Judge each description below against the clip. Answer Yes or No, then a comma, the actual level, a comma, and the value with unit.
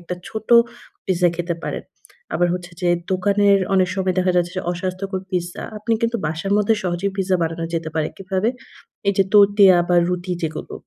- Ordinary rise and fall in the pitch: No, narrow, 2.2 semitones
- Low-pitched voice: No, medium, 185 Hz